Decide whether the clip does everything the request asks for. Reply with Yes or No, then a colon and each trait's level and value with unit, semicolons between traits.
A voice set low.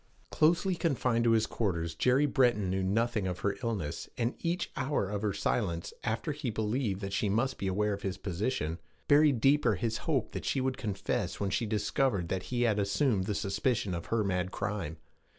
Yes: low, 105 Hz